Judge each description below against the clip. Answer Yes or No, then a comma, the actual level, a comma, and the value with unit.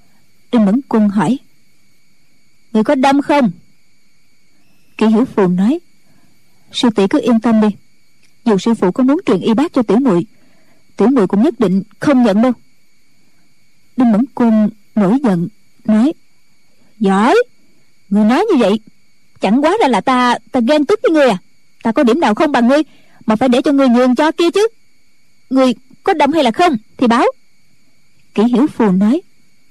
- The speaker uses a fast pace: No, average, 180 wpm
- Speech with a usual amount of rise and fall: Yes, average, 4.5 semitones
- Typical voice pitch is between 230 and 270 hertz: Yes, high, 240 Hz